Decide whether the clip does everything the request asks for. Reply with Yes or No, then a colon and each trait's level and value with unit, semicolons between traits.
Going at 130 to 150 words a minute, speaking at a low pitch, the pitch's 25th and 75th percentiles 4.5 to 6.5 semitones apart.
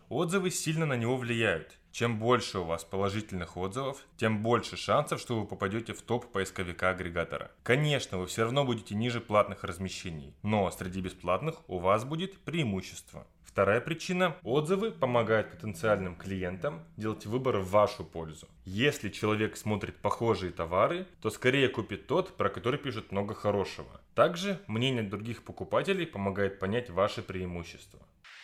Yes: average, 145 wpm; low, 110 Hz; average, 5.1 semitones